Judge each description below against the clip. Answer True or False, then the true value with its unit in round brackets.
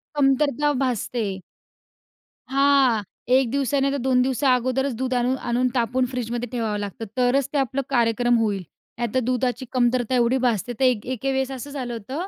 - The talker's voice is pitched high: True (255 Hz)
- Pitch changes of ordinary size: False (2.0 semitones)